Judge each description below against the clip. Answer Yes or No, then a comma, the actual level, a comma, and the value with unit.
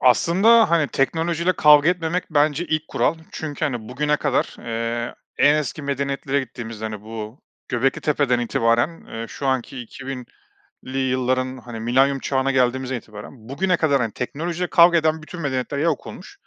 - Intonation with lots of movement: No, average, 4.1 semitones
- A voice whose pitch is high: No, low, 135 Hz